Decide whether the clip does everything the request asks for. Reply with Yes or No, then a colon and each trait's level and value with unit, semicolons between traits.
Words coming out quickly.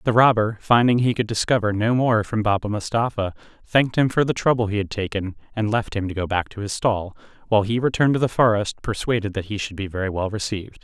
Yes: fast, 235 wpm